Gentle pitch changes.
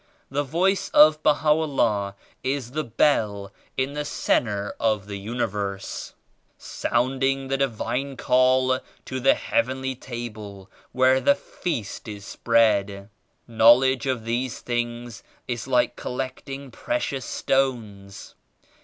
No: average, 3.7 semitones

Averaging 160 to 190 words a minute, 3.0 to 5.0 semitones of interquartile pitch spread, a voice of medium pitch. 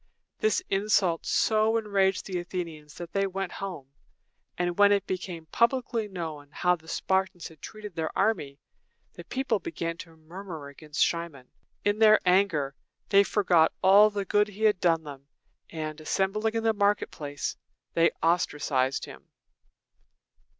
No: average, 150 wpm; average, 4.2 semitones; medium, 180 Hz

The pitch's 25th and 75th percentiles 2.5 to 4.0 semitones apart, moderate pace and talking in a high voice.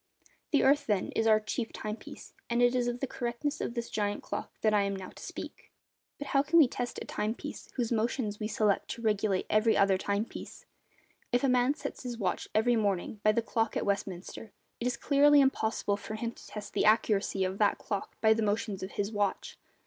No: average, 2.9 semitones; fast, 225 wpm; high, 220 Hz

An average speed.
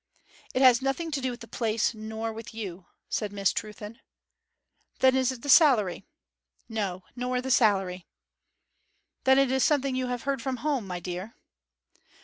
Yes: average, 165 wpm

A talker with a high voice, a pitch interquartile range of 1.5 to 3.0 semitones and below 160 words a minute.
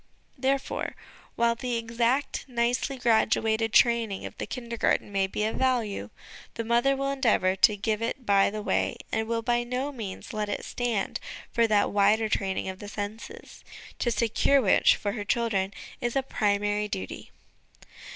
No: high, 225 Hz; average, 2.7 semitones; average, 180 wpm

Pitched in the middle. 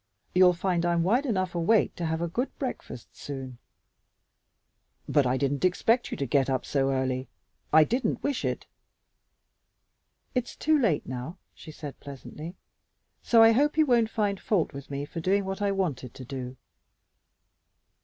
Yes: medium, 170 Hz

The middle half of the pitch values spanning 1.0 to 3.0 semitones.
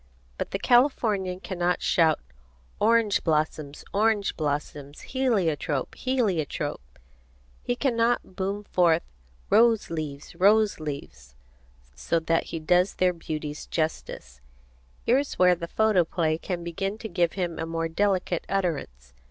No: average, 4.6 semitones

